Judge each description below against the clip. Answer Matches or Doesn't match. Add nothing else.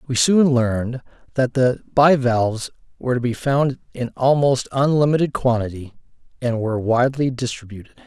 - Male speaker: Matches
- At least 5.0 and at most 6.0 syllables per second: Matches